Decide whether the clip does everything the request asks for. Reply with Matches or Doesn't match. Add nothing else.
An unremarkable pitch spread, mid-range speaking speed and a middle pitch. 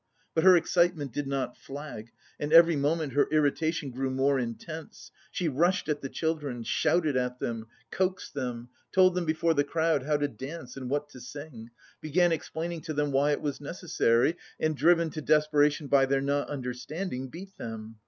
Matches